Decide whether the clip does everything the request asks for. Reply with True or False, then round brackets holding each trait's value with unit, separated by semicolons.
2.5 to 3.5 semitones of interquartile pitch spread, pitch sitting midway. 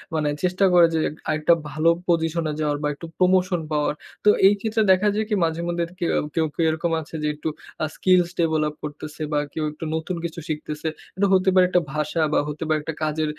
True (2.9 semitones; 165 Hz)